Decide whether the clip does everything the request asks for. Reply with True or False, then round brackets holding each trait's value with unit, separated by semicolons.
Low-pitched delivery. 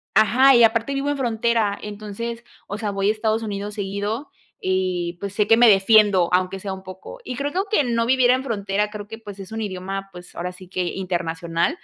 False (205 Hz)